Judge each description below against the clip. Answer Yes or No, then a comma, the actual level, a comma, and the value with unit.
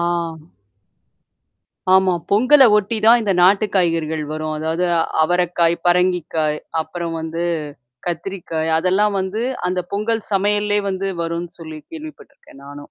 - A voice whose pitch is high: No, medium, 180 Hz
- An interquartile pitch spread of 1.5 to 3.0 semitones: No, average, 4.0 semitones